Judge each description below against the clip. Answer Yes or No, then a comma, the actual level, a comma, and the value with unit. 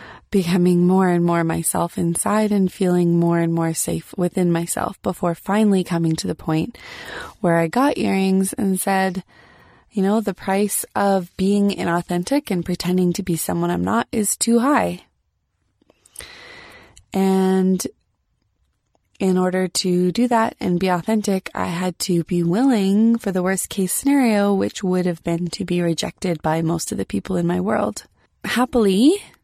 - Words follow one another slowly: No, average, 160 wpm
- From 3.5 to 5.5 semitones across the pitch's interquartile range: No, average, 2.8 semitones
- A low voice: No, medium, 185 Hz